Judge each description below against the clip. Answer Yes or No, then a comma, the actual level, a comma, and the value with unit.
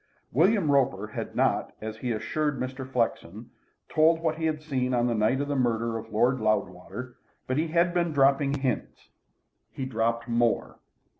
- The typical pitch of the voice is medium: No, low, 130 Hz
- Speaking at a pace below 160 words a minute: No, average, 175 wpm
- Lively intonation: No, average, 4.4 semitones